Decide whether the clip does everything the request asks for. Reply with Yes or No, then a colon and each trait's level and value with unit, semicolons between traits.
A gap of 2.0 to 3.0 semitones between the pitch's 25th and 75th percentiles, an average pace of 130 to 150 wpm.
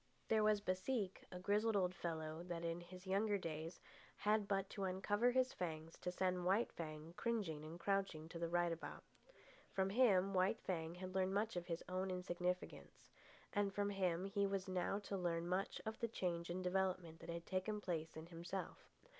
No: average, 2.7 semitones; average, 190 wpm